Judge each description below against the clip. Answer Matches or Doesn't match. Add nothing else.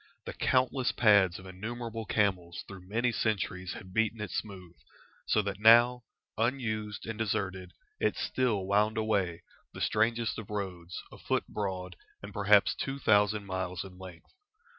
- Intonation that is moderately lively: Matches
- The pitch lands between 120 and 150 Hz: Doesn't match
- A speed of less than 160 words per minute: Matches